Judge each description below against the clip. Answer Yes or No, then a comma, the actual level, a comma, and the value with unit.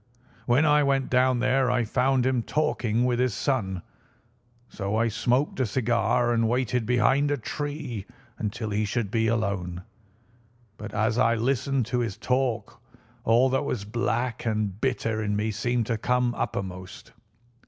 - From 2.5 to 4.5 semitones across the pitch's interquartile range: Yes, average, 2.9 semitones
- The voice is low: Yes, low, 120 Hz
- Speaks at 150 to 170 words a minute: Yes, average, 155 wpm